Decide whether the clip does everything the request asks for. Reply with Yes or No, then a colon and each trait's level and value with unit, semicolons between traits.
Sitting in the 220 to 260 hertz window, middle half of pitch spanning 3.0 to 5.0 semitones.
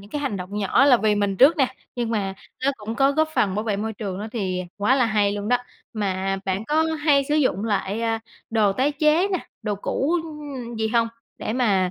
No: high, 225 Hz; wide, 5.5 semitones